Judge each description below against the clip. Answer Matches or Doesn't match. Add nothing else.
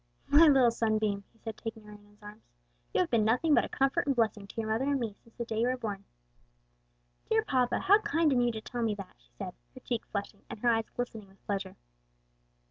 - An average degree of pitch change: Matches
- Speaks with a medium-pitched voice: Doesn't match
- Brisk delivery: Matches